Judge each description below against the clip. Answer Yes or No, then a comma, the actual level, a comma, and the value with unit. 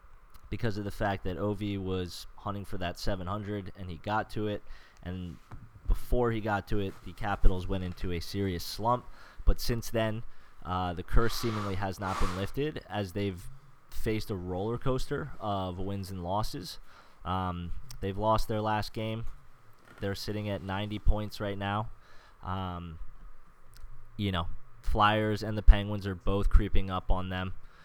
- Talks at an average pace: Yes, average, 165 wpm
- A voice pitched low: Yes, low, 100 Hz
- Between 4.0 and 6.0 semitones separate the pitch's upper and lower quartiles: No, average, 2.7 semitones